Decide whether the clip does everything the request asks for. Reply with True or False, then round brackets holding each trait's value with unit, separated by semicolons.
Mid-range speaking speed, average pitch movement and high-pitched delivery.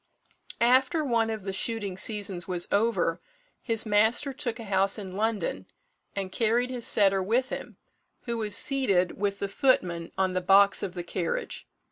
True (165 wpm; 3.5 semitones; 205 Hz)